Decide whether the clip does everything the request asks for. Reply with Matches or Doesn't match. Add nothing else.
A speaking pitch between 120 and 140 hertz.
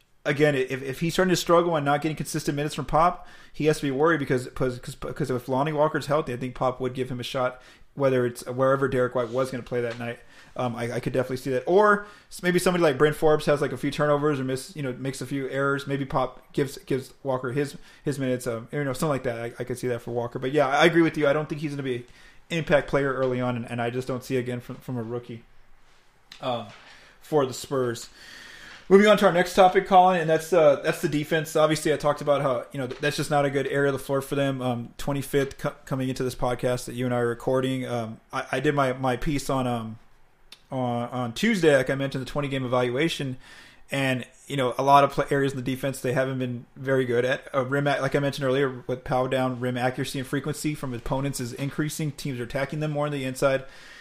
Matches